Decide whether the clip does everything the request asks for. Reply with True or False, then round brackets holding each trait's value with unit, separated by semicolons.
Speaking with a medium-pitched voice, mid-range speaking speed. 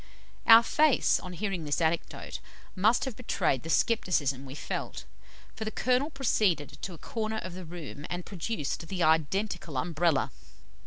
True (180 Hz; 155 wpm)